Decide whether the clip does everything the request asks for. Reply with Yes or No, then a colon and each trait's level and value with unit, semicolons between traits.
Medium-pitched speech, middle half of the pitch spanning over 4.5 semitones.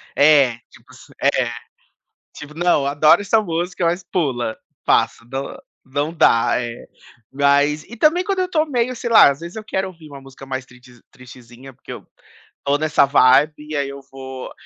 Yes: medium, 145 Hz; average, 5.0 semitones